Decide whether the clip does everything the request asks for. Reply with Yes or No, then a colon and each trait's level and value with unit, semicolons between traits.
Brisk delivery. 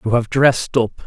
Yes: fast, 225 wpm